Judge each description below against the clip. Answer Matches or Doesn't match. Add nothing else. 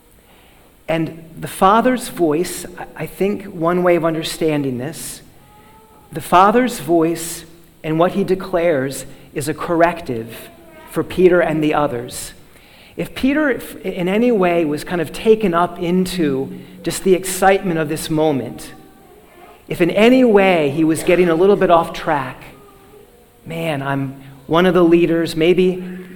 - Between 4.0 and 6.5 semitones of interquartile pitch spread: Doesn't match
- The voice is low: Doesn't match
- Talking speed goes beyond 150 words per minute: Doesn't match